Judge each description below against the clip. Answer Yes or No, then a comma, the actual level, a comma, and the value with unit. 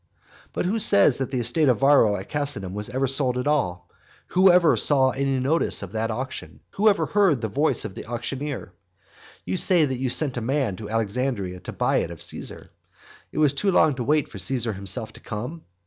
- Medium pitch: No, low, 130 Hz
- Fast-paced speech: Yes, fast, 210 wpm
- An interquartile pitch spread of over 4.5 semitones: Yes, average, 5.0 semitones